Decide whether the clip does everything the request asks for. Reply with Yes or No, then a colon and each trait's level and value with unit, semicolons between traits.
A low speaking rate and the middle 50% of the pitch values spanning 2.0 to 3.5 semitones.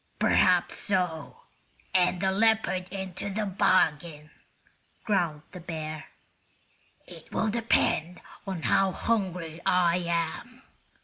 Yes: slow, 105 wpm; average, 2.9 semitones